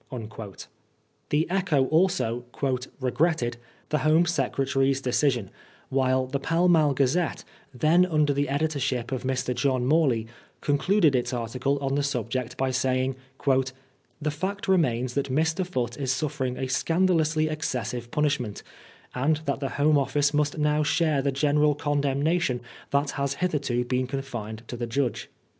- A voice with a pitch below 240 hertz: Yes, medium, 140 Hz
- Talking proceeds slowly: No, average, 150 wpm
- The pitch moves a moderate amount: Yes, average, 3.1 semitones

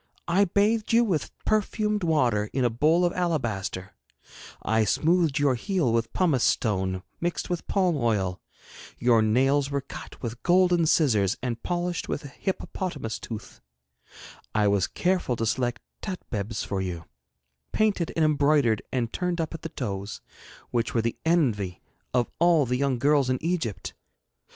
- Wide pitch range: Yes, wide, 7.5 semitones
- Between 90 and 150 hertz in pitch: Yes, low, 135 Hz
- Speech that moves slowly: No, average, 155 wpm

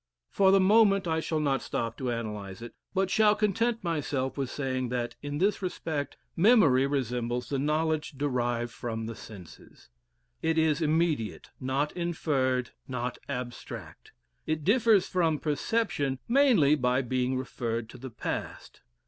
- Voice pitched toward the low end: No, medium, 145 Hz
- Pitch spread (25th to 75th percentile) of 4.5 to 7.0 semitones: Yes, wide, 5.5 semitones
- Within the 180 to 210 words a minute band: No, average, 145 wpm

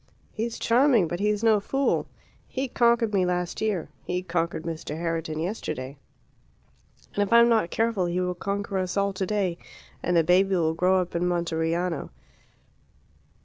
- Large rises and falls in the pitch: No, average, 3.7 semitones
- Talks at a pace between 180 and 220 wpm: No, average, 160 wpm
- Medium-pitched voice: Yes, medium, 180 Hz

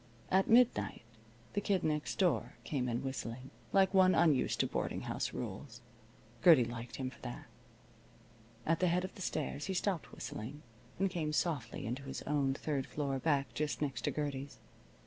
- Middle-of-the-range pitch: Yes, medium, 145 Hz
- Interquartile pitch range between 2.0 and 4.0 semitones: No, average, 5.2 semitones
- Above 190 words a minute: No, average, 170 wpm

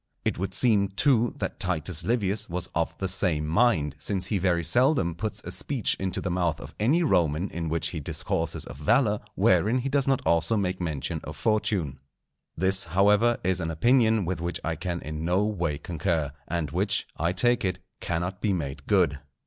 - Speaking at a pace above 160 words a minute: Yes, average, 190 wpm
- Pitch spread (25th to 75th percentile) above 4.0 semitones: Yes, average, 4.5 semitones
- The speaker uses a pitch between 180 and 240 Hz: No, very low, 95 Hz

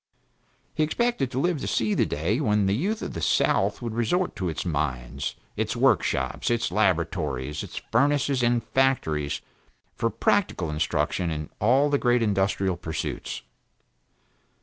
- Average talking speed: Yes, average, 150 wpm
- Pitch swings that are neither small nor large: No, wide, 8.9 semitones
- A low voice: Yes, low, 105 Hz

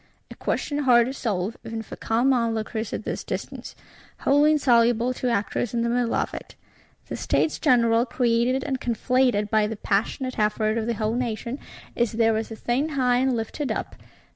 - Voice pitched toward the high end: Yes, high, 235 Hz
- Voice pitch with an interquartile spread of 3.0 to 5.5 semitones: No, narrow, 2.4 semitones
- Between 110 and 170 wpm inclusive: No, average, 190 wpm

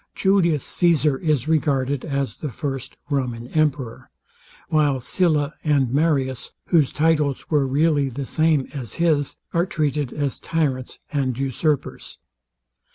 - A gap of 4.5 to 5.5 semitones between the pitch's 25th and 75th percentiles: No, average, 2.8 semitones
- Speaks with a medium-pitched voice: Yes, medium, 145 Hz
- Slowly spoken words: Yes, slow, 125 wpm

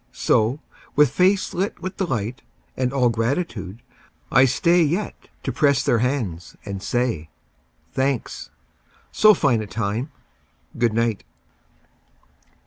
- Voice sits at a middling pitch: No, low, 125 Hz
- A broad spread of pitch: No, average, 4.7 semitones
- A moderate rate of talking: No, slow, 120 wpm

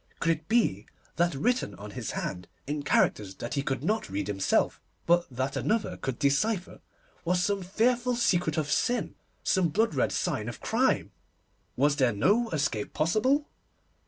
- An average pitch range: No, wide, 8.1 semitones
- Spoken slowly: No, average, 160 wpm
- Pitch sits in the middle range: Yes, medium, 160 Hz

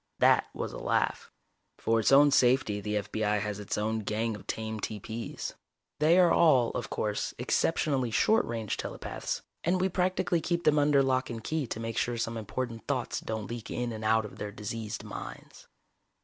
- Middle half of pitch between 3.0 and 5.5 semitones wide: Yes, average, 4.4 semitones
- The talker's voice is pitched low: Yes, low, 115 Hz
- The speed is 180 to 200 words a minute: Yes, average, 185 wpm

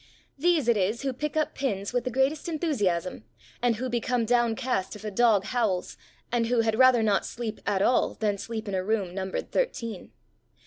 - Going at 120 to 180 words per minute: No, average, 190 wpm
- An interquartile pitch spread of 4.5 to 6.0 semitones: No, average, 3.8 semitones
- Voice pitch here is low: No, high, 230 Hz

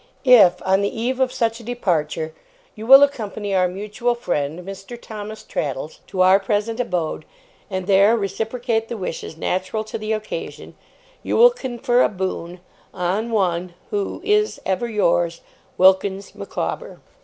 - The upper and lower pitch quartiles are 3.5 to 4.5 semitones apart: Yes, average, 4.2 semitones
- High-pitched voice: Yes, high, 205 Hz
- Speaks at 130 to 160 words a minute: Yes, average, 150 wpm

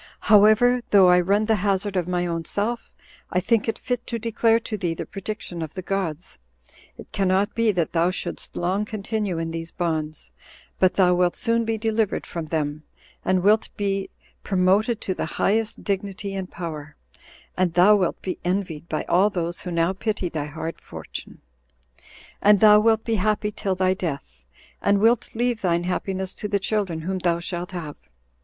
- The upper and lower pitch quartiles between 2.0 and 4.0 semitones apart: Yes, average, 3.5 semitones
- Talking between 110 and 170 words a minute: No, average, 180 wpm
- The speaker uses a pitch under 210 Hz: Yes, high, 190 Hz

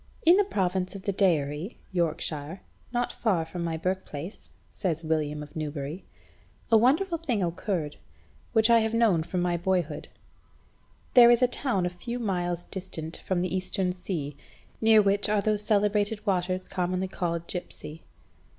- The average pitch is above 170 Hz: Yes, medium, 185 Hz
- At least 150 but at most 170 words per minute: Yes, average, 155 wpm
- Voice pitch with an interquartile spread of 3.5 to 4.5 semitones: Yes, average, 3.9 semitones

